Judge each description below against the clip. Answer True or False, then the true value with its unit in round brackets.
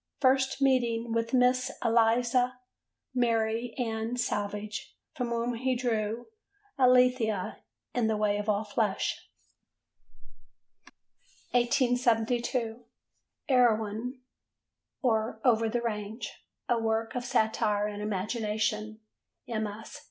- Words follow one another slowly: True (95 wpm)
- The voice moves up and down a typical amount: False (2.3 semitones)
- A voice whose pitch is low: False (230 Hz)